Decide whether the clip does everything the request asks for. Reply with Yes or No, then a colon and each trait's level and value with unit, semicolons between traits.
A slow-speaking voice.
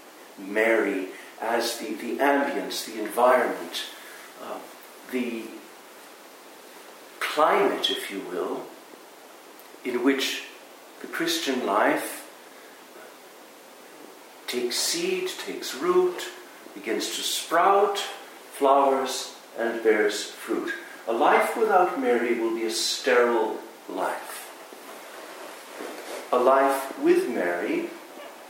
Yes: slow, 90 wpm